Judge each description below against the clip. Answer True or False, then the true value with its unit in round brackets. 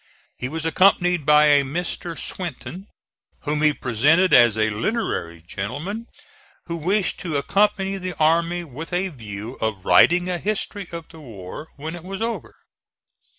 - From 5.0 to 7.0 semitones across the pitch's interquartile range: True (5.6 semitones)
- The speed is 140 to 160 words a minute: True (150 wpm)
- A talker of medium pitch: True (160 Hz)